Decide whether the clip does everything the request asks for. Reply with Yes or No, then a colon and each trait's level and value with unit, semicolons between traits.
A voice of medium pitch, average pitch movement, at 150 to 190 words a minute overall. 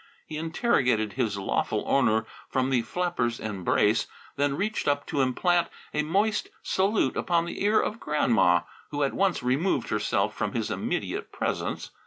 No: medium, 145 Hz; wide, 6.9 semitones; average, 155 wpm